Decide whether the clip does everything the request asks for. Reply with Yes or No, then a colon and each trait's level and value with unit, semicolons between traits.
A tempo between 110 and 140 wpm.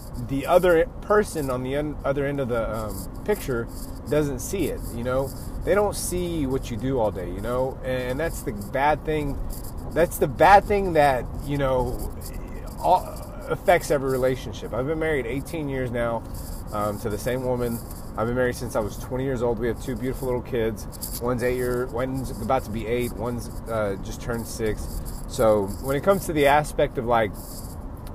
No: average, 190 wpm